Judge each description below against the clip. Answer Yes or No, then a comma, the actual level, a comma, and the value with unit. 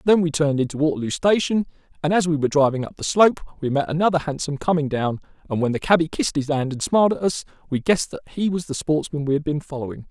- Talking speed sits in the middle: No, fast, 250 wpm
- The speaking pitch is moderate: Yes, medium, 155 Hz